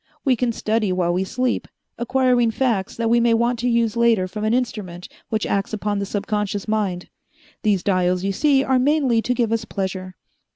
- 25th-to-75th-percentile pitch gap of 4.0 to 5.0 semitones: No, average, 3.6 semitones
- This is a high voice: Yes, high, 220 Hz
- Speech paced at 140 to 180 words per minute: No, average, 195 wpm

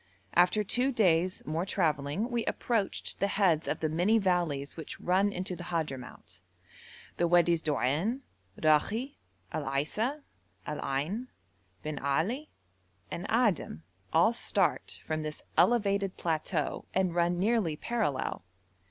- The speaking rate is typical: No, slow, 125 wpm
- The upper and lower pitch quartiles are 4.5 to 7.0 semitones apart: Yes, wide, 5.4 semitones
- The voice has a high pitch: No, medium, 175 Hz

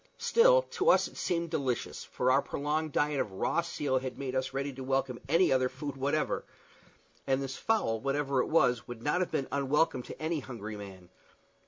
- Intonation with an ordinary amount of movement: Yes, average, 3.2 semitones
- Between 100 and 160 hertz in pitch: Yes, low, 135 Hz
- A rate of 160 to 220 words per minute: Yes, average, 195 wpm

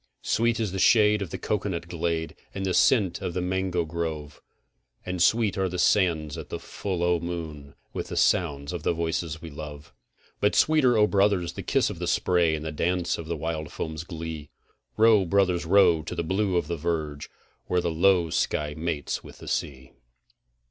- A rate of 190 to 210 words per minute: Yes, average, 195 wpm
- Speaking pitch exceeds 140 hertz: No, very low, 85 Hz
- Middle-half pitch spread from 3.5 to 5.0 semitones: No, average, 3.1 semitones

